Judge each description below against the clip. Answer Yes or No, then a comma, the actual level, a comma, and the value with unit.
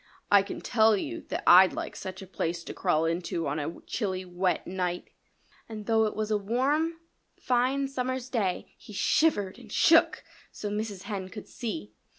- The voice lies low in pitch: No, high, 205 Hz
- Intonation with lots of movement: No, average, 4.2 semitones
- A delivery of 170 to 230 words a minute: Yes, average, 175 wpm